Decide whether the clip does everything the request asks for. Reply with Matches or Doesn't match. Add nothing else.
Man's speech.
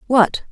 Doesn't match